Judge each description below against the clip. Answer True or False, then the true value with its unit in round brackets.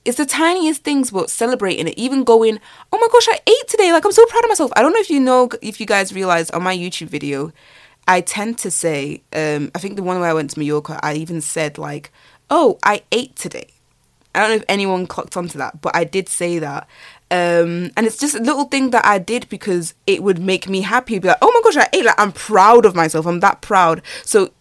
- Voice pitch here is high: True (195 Hz)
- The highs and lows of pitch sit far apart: True (6.7 semitones)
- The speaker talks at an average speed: False (250 wpm)